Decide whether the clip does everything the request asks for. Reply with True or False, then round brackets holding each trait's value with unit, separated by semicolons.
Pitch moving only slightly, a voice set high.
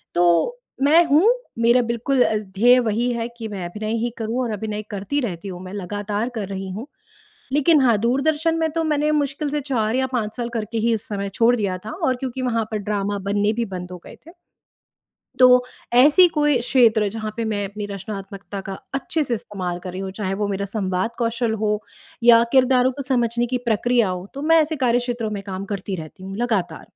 False (4.0 semitones; 225 Hz)